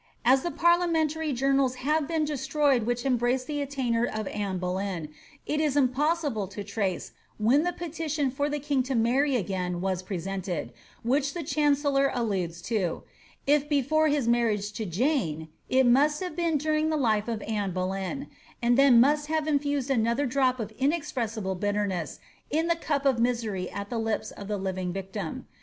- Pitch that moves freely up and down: Yes, wide, 6.2 semitones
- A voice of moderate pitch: No, very high, 255 Hz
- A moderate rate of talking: Yes, average, 175 wpm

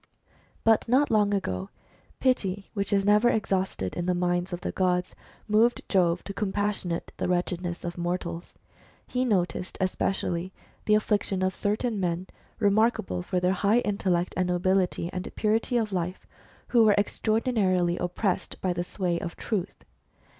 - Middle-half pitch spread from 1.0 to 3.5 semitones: Yes, average, 3.1 semitones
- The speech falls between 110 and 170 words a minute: Yes, average, 155 wpm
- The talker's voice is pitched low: No, high, 190 Hz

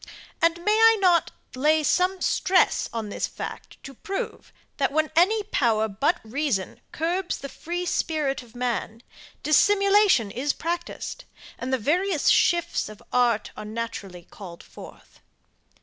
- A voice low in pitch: No, very high, 295 Hz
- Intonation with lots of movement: Yes, wide, 7.6 semitones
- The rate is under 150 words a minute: Yes, average, 140 wpm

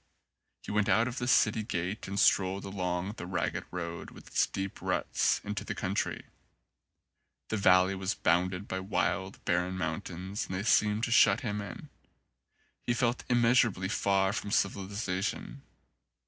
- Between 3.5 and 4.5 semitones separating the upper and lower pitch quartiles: No, narrow, 2.4 semitones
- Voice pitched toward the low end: Yes, low, 100 Hz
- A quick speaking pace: No, average, 160 wpm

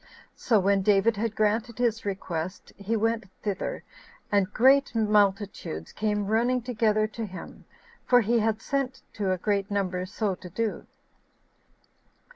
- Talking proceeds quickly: No, average, 140 wpm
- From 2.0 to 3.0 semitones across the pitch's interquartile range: Yes, narrow, 2.6 semitones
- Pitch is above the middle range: Yes, high, 210 Hz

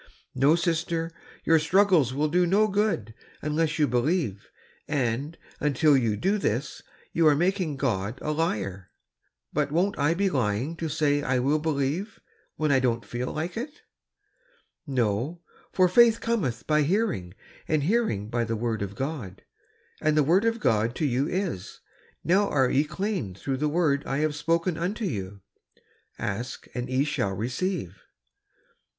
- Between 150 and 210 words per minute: Yes, average, 160 wpm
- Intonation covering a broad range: Yes, wide, 6.0 semitones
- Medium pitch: Yes, medium, 150 Hz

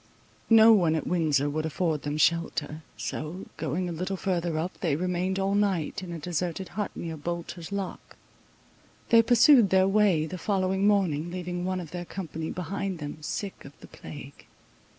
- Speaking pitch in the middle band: Yes, medium, 175 Hz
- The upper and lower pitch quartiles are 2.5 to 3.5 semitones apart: Yes, average, 3.2 semitones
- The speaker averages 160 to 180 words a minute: Yes, average, 170 wpm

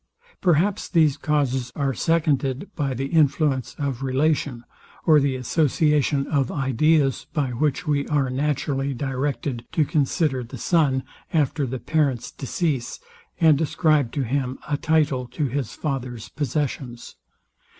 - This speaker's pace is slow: Yes, slow, 130 wpm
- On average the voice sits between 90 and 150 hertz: Yes, medium, 140 Hz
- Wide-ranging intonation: No, average, 2.7 semitones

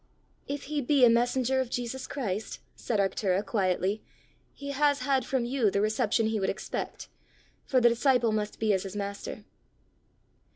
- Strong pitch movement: No, average, 4.3 semitones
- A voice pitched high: Yes, high, 230 Hz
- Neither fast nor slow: Yes, average, 165 wpm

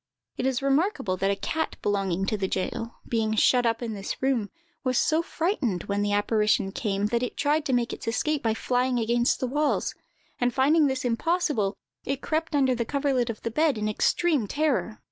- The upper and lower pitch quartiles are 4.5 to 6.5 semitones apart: Yes, average, 4.9 semitones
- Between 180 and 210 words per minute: Yes, average, 200 wpm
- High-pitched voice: Yes, high, 245 Hz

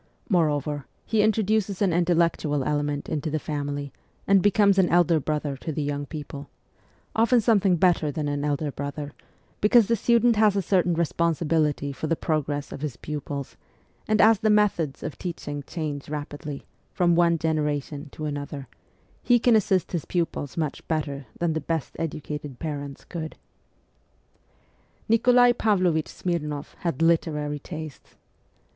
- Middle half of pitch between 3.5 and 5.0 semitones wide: Yes, average, 4.0 semitones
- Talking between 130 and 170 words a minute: Yes, average, 150 wpm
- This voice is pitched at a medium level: Yes, medium, 160 Hz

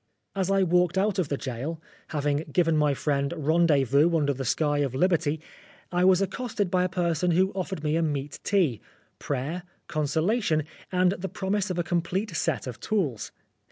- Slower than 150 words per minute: No, average, 180 wpm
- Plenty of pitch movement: No, average, 4.2 semitones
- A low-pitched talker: No, medium, 165 Hz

